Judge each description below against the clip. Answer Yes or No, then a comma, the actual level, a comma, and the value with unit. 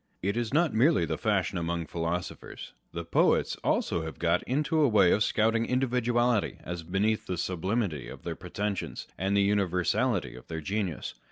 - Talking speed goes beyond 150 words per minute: Yes, average, 180 wpm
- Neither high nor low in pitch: No, low, 100 Hz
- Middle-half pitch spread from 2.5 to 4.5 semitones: No, average, 5.0 semitones